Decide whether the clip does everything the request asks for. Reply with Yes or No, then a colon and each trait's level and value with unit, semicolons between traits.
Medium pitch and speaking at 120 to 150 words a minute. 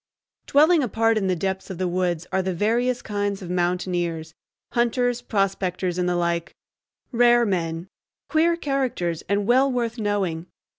No: high, 195 Hz; average, 140 wpm